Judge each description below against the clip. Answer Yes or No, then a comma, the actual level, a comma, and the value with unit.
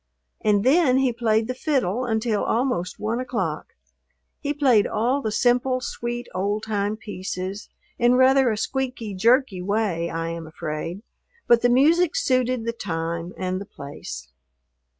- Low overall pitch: No, high, 225 Hz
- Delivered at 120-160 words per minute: Yes, average, 150 wpm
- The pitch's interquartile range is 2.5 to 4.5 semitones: No, average, 5.2 semitones